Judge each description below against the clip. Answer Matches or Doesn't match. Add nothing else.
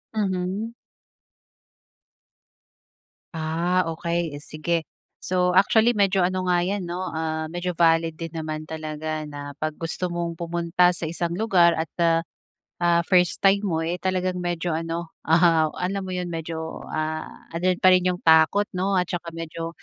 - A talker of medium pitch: Matches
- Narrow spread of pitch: Matches